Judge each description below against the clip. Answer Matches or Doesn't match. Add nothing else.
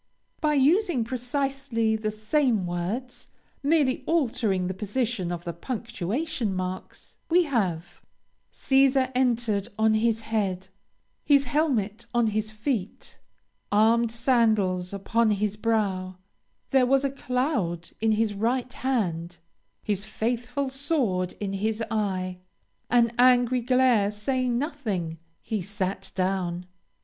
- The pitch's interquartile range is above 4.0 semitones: Matches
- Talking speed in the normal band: Doesn't match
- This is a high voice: Matches